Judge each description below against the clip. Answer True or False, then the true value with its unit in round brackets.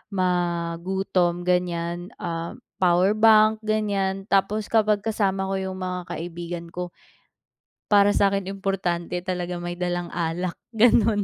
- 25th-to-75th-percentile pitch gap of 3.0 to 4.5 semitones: False (2.4 semitones)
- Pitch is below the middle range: False (185 Hz)